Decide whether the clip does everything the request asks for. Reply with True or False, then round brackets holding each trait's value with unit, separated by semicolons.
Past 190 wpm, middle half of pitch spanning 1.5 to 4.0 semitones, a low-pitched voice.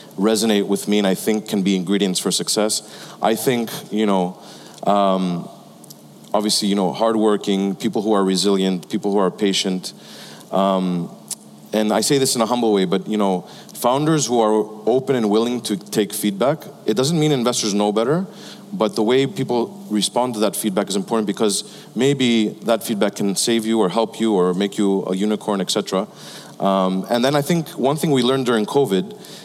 False (185 wpm; 3.6 semitones; 110 Hz)